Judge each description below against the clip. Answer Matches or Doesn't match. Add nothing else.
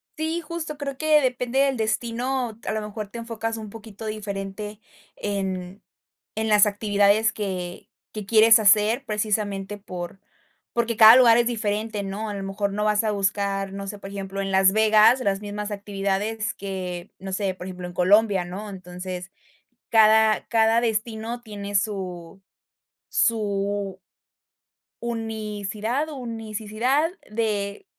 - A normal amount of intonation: Doesn't match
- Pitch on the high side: Matches